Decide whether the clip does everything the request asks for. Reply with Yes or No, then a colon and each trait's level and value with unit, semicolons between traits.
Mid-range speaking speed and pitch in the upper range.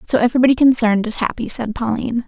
Yes: average, 185 wpm; high, 235 Hz